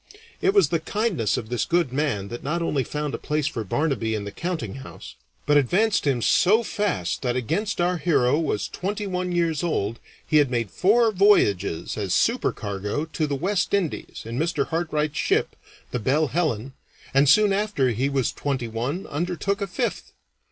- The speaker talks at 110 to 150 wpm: No, average, 180 wpm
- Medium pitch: Yes, medium, 150 Hz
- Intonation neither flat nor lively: No, wide, 6.7 semitones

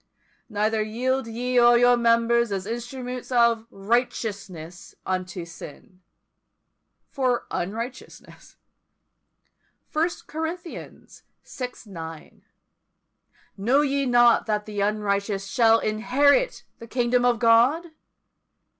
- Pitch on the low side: No, high, 235 Hz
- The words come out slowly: Yes, slow, 95 wpm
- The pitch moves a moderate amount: Yes, average, 3.2 semitones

